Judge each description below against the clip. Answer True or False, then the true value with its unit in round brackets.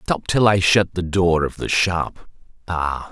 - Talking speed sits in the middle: True (190 wpm)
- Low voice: True (90 Hz)